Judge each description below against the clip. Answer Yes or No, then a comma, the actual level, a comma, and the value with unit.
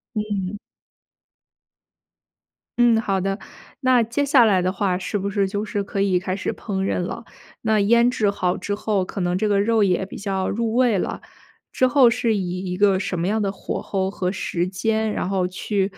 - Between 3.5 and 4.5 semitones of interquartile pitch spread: No, average, 2.7 semitones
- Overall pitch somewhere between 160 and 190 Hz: No, high, 200 Hz